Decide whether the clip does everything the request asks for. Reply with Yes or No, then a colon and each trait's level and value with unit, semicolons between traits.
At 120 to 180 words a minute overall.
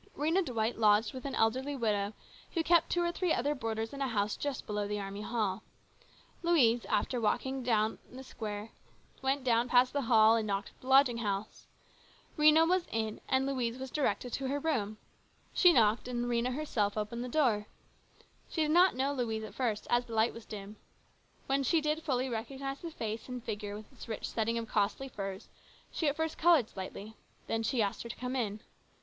No: average, 200 wpm